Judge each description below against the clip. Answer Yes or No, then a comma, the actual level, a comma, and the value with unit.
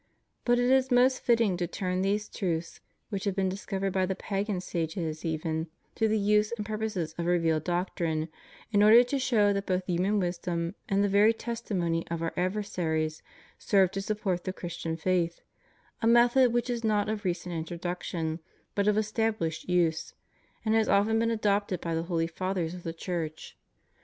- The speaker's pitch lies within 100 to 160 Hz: No, high, 190 Hz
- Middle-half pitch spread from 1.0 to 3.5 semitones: No, average, 4.0 semitones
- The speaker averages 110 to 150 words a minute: No, average, 180 wpm